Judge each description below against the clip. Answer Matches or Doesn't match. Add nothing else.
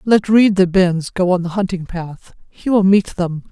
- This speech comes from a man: Doesn't match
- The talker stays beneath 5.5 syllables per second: Matches